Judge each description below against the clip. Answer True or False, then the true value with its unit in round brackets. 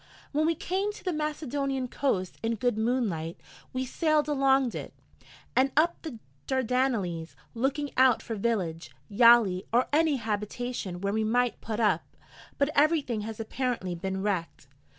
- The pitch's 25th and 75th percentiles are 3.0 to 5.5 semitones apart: True (4.9 semitones)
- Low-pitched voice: False (245 Hz)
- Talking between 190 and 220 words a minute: False (150 wpm)